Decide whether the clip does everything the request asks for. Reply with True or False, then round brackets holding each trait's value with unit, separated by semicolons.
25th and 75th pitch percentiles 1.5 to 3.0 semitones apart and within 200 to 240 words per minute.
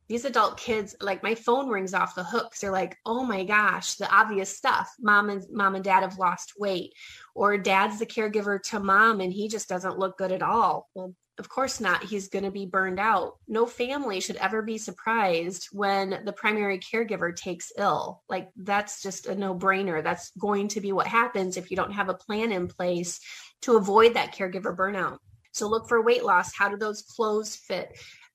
True (2.7 semitones; 205 wpm)